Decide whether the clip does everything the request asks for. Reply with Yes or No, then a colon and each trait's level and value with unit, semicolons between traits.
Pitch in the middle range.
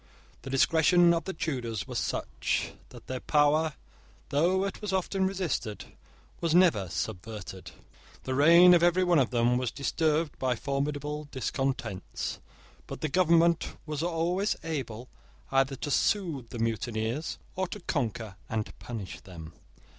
Yes: medium, 145 Hz